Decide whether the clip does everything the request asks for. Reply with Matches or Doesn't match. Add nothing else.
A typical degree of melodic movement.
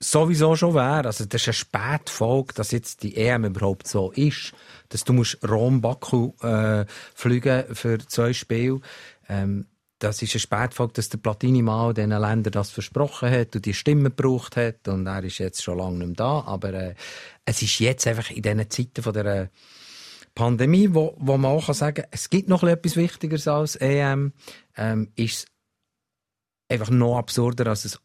Matches